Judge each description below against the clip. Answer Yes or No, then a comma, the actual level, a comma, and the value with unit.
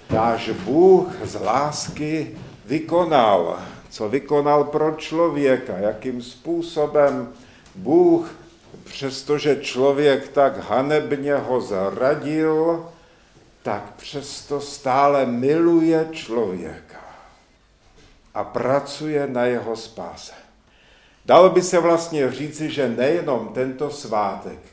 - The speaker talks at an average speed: No, slow, 90 wpm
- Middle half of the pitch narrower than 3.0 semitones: No, average, 3.3 semitones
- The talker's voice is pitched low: No, medium, 145 Hz